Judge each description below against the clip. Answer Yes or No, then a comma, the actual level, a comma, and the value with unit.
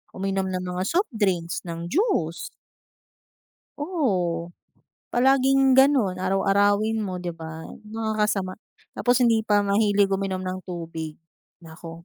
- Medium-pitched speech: No, high, 195 Hz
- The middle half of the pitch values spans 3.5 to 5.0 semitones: Yes, average, 3.9 semitones